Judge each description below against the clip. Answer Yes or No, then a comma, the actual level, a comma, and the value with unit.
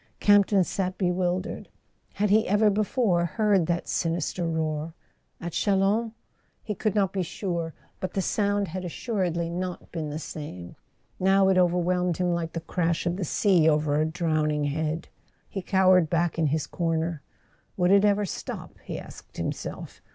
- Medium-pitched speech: Yes, medium, 180 Hz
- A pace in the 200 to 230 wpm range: No, average, 165 wpm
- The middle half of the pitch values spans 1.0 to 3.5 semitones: Yes, average, 3.1 semitones